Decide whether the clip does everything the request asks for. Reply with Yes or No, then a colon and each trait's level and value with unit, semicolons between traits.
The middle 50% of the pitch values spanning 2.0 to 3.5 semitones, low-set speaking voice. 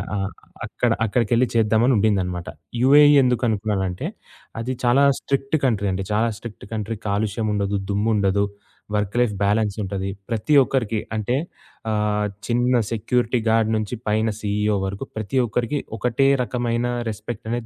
Yes: average, 2.9 semitones; low, 110 Hz